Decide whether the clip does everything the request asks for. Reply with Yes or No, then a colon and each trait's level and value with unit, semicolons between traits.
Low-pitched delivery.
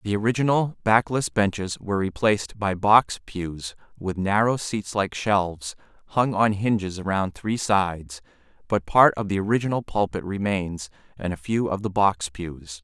Yes: low, 100 Hz